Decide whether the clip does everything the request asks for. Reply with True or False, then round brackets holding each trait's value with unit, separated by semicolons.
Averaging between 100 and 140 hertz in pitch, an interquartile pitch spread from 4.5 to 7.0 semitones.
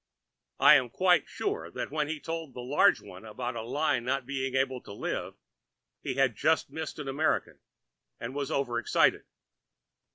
False (135 Hz; 3.5 semitones)